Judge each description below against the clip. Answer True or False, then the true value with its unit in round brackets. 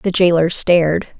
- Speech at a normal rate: True (150 wpm)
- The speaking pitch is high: False (170 Hz)